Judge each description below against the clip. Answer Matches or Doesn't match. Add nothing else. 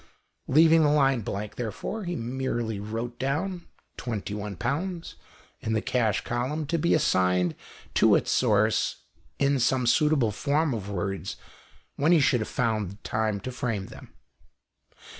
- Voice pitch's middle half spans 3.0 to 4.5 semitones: Doesn't match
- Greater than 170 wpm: Doesn't match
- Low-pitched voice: Matches